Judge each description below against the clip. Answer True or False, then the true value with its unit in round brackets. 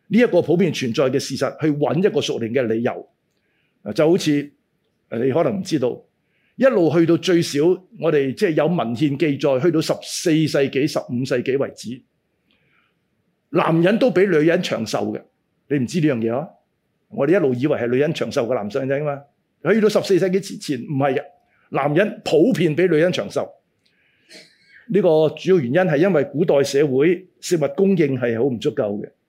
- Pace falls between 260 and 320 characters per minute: True (270 characters per minute)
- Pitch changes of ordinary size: True (4.7 semitones)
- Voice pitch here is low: False (155 Hz)